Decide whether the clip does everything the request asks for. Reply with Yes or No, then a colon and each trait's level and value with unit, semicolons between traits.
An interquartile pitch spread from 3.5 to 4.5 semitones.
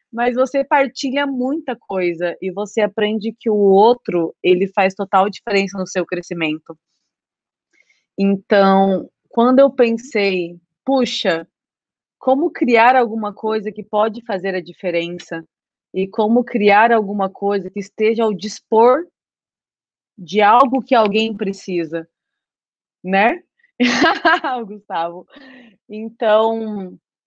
Yes: average, 4.1 semitones